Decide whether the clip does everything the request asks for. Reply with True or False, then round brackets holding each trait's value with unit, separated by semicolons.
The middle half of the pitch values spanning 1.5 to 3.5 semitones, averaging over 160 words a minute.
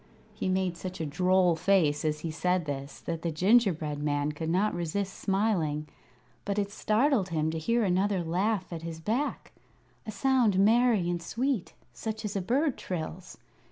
False (4.5 semitones; 170 wpm)